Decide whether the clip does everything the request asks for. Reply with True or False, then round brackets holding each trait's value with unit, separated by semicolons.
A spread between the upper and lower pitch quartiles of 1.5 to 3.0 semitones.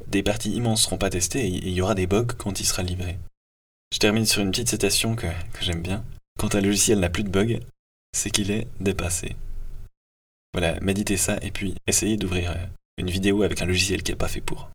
True (2.5 semitones)